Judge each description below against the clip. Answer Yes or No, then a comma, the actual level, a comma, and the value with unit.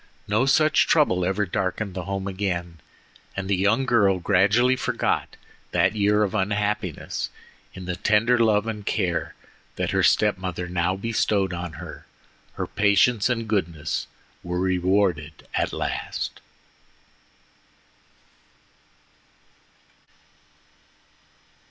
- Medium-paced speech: No, slow, 110 wpm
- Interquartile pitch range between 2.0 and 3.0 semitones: Yes, average, 2.7 semitones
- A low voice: Yes, low, 100 Hz